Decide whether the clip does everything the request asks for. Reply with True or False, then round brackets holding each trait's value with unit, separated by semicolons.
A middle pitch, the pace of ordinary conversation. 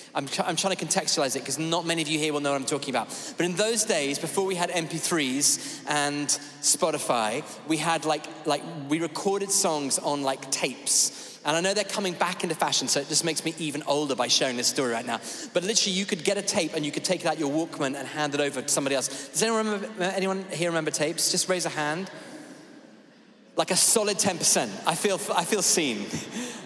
False (165 Hz; 230 wpm)